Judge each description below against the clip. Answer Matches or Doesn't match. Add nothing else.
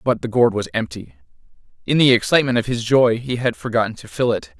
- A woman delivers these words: Doesn't match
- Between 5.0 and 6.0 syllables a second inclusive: Doesn't match